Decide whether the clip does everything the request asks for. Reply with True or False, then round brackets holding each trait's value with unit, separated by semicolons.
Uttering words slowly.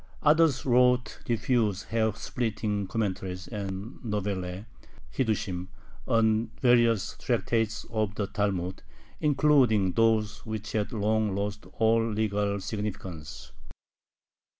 True (100 wpm)